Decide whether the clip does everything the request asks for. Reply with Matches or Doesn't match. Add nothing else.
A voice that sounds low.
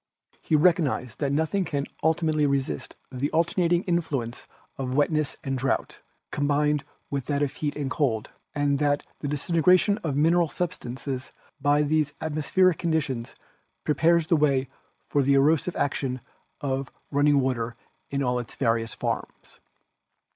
Doesn't match